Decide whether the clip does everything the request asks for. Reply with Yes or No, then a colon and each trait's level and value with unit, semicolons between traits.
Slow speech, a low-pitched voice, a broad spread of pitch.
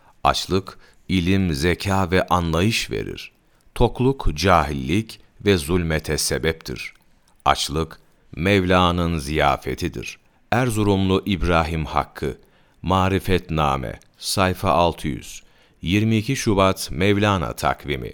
No: slow, 80 wpm; very low, 90 Hz; average, 3.8 semitones